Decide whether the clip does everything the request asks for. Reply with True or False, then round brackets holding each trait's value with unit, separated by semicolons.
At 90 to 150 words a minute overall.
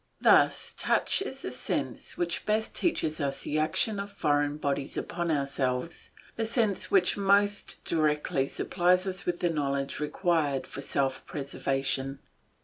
True (140 wpm)